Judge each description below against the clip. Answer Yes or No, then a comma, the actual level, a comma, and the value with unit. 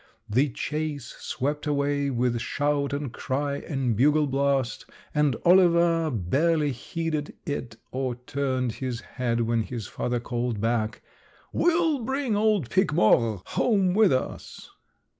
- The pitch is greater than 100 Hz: Yes, medium, 140 Hz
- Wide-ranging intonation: No, average, 4.3 semitones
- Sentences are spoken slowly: Yes, slow, 130 wpm